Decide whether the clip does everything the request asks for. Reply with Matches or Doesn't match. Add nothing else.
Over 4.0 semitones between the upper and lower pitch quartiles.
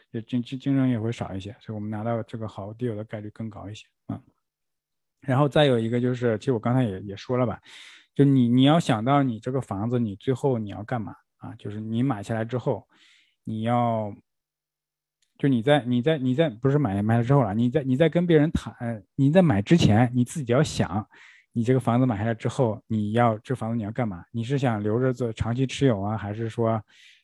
Doesn't match